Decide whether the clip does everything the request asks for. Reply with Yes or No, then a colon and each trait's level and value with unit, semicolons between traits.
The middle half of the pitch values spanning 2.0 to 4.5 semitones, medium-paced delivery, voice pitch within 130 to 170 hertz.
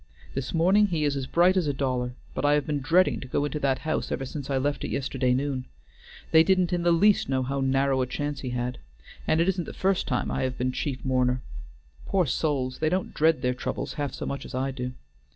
No: average, 4.0 semitones; fast, 240 wpm; medium, 140 Hz